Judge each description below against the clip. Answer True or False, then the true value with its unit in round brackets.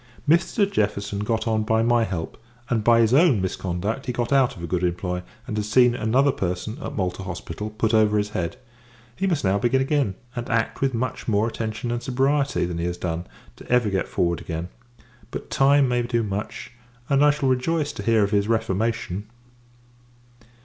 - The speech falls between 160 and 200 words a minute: True (195 wpm)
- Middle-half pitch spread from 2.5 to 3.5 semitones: False (4.3 semitones)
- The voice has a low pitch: True (110 Hz)